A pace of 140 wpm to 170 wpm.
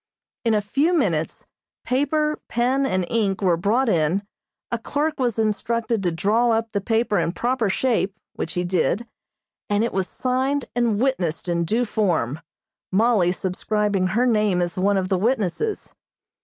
Yes: average, 160 wpm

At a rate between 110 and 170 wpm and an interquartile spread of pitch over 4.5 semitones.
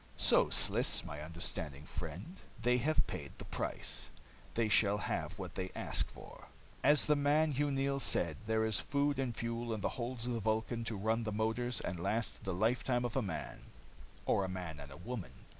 No: average, 195 wpm; average, 4.9 semitones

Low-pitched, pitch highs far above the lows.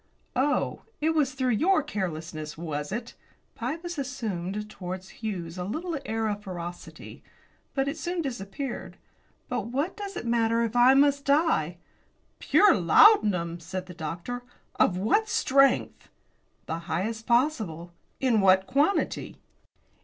No: high, 225 Hz; wide, 7.6 semitones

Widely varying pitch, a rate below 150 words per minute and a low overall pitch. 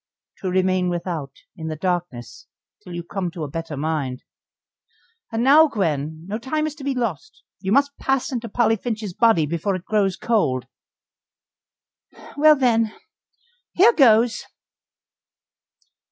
No: wide, 6.4 semitones; average, 140 wpm; high, 195 Hz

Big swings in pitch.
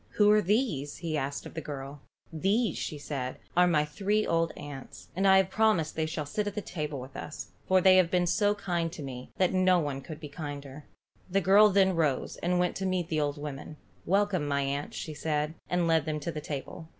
No: average, 4.4 semitones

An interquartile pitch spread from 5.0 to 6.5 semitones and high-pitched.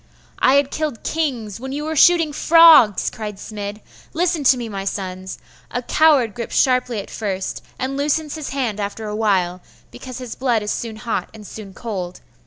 Yes: average, 5.3 semitones; high, 235 Hz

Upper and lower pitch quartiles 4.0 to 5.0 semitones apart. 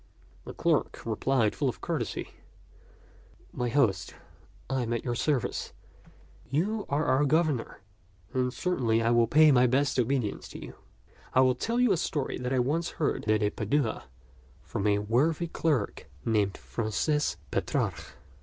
Yes: average, 4.7 semitones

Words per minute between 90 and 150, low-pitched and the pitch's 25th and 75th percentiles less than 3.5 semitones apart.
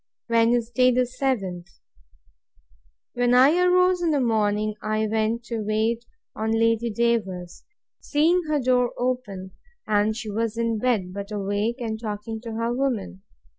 No: average, 140 wpm; high, 230 Hz; average, 2.7 semitones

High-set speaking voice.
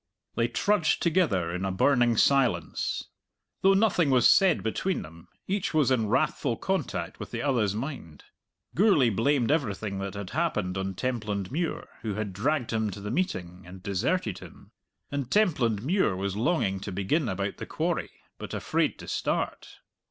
No: low, 115 Hz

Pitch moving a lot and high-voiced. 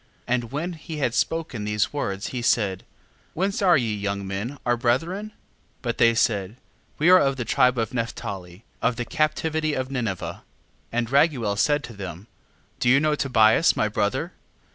No: wide, 5.8 semitones; low, 120 Hz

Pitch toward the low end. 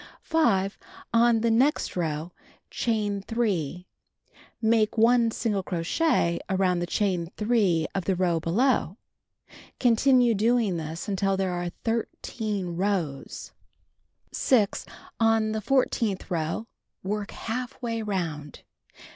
No: high, 205 Hz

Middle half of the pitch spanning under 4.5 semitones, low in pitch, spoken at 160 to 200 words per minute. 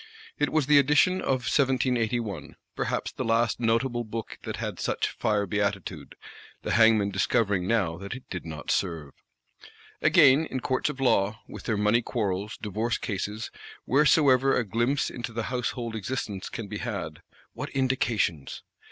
No: average, 4.0 semitones; low, 115 Hz; average, 150 wpm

